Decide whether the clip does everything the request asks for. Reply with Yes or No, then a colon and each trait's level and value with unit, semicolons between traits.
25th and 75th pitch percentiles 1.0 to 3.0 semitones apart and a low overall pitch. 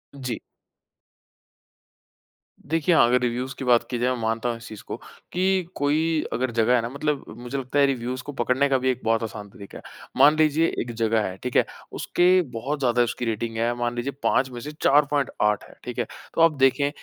No: average, 3.4 semitones; low, 125 Hz